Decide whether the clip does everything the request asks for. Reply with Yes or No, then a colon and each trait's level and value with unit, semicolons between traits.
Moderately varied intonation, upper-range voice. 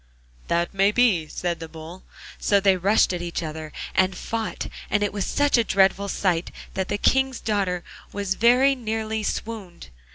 Yes: average, 3.8 semitones; high, 195 Hz